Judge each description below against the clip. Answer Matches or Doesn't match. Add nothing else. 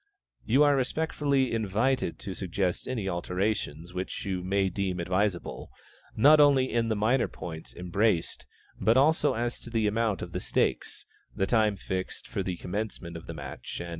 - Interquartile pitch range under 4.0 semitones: Doesn't match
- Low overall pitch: Matches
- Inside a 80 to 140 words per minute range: Doesn't match